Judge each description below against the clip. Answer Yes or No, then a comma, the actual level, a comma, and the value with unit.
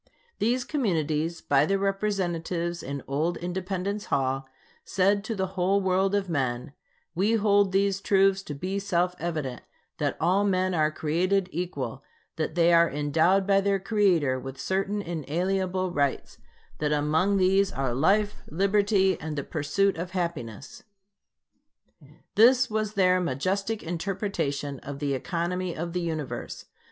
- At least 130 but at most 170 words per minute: Yes, average, 140 wpm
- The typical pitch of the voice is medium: Yes, medium, 180 Hz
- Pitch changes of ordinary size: Yes, average, 4.2 semitones